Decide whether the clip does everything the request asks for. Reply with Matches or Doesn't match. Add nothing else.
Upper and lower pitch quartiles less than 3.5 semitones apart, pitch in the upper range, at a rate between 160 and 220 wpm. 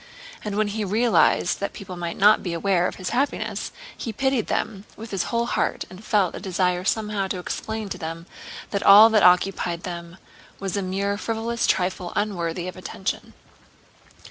Matches